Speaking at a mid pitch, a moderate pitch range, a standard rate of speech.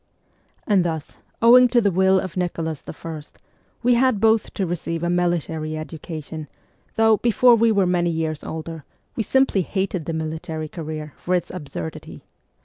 Yes: medium, 175 Hz; average, 4.4 semitones; average, 155 wpm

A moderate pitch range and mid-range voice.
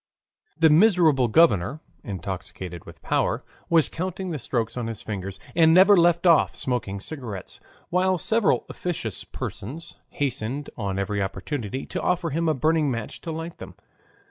No: wide, 7.6 semitones; medium, 145 Hz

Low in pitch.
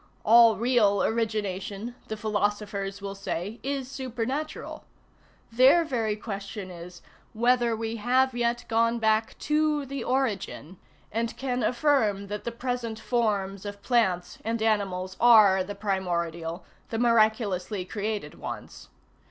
No: high, 220 Hz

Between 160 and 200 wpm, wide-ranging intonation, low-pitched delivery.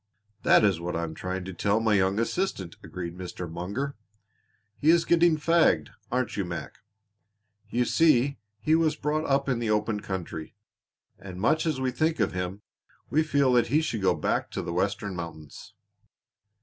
Yes: average, 175 wpm; wide, 8.0 semitones; low, 110 Hz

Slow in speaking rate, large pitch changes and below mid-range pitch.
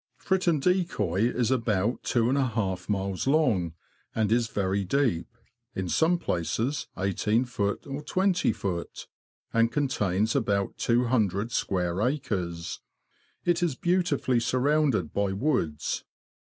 Yes: slow, 115 wpm; wide, 6.1 semitones; low, 115 Hz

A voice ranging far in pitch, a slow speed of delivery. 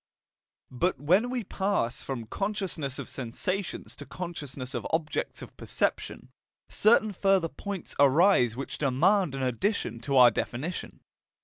Yes: wide, 7.1 semitones; slow, 130 wpm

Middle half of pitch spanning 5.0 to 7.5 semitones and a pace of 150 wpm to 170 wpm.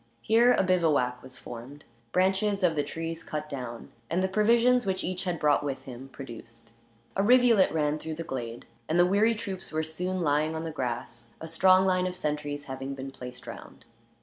No: wide, 5.5 semitones; average, 195 wpm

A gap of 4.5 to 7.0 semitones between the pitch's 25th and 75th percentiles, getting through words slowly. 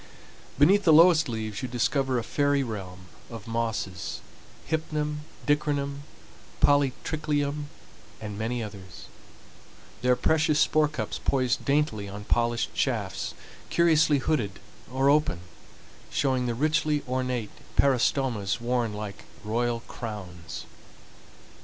Yes: average, 5.2 semitones; slow, 105 wpm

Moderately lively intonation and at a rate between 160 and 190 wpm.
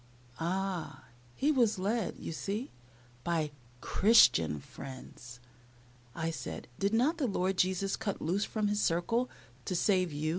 No: average, 4.8 semitones; average, 140 wpm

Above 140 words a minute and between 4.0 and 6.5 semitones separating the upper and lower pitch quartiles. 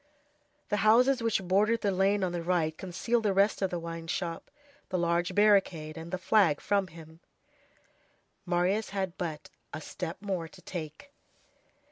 No: average, 160 wpm; average, 3.3 semitones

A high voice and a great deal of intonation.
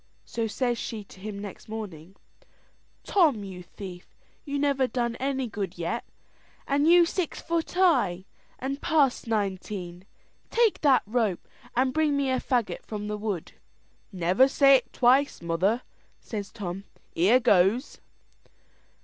Yes: high, 230 Hz; wide, 5.9 semitones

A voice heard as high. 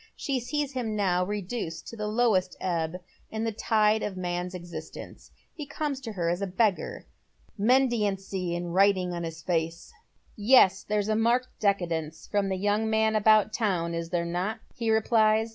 Yes: high, 205 Hz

